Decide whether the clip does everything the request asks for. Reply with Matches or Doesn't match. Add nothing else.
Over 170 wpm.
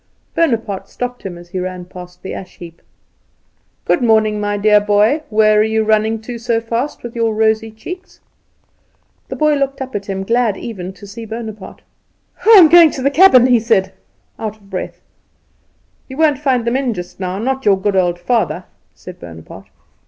Matches